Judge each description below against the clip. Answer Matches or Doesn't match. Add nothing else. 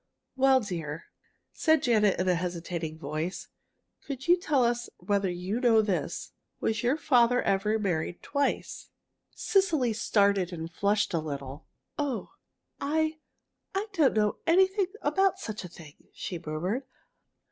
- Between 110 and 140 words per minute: Matches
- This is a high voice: Matches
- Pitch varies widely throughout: Matches